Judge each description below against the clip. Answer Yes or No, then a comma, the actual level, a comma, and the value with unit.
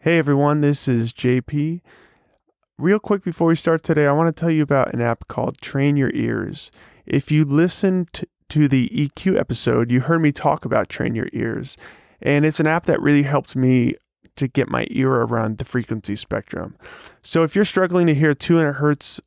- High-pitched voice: No, medium, 145 Hz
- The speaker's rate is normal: Yes, average, 195 wpm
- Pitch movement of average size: Yes, average, 4.1 semitones